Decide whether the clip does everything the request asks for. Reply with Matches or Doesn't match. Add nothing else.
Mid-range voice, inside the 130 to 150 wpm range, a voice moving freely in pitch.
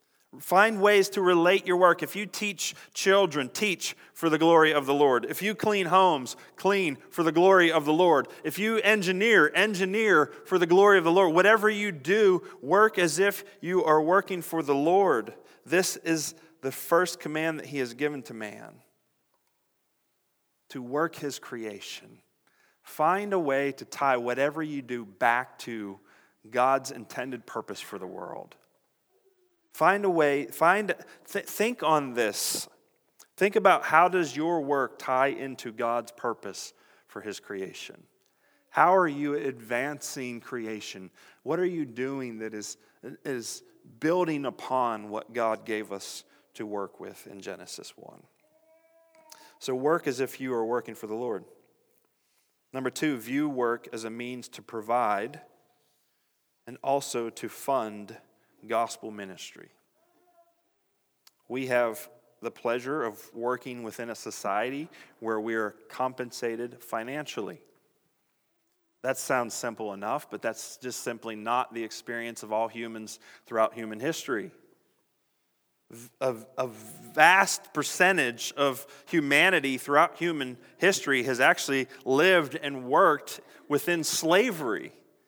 Matches